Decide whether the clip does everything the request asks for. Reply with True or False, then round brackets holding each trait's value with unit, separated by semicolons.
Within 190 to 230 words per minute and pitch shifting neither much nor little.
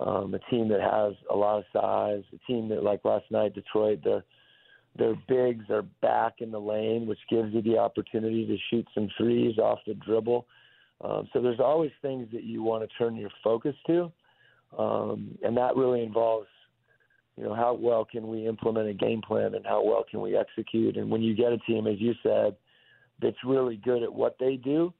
False (205 wpm; 2.1 semitones)